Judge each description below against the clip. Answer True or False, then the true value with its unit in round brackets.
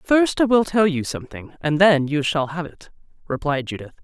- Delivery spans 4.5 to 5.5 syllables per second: True (5.1 syllables/s)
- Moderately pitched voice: True (165 Hz)